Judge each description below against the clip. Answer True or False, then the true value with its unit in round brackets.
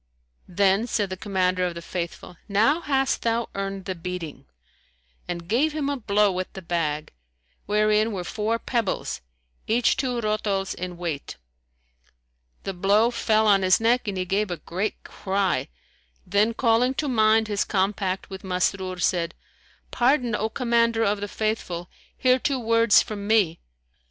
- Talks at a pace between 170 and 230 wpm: False (155 wpm)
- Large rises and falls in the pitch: False (3.7 semitones)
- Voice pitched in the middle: False (205 Hz)